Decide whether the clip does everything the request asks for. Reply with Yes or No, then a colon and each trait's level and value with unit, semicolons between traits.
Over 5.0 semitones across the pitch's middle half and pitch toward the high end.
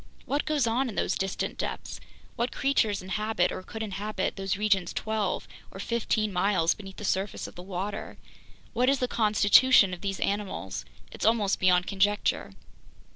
No: narrow, 2.5 semitones; high, 205 Hz